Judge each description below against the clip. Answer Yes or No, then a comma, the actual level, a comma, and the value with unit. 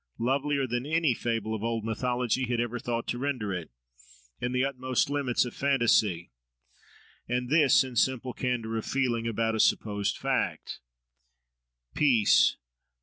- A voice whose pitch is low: Yes, low, 120 Hz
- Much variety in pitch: No, narrow, 2.6 semitones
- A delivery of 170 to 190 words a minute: No, average, 145 wpm